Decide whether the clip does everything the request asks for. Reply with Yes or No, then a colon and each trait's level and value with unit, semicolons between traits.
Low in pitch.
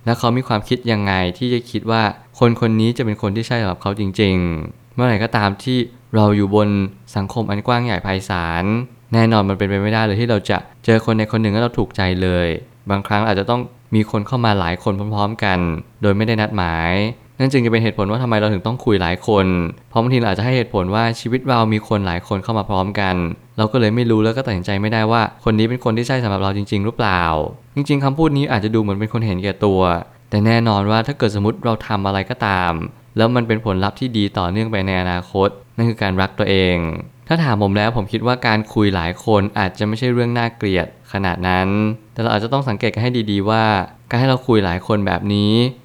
Yes: low, 110 Hz